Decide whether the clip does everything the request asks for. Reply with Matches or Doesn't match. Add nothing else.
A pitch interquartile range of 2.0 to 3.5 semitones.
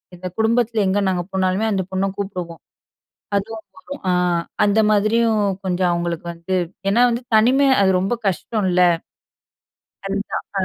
Matches